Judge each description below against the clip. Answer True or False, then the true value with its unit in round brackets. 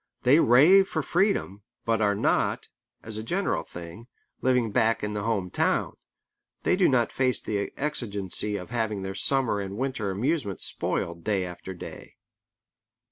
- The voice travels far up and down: False (4.7 semitones)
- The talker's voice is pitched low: True (110 Hz)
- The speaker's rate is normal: True (155 wpm)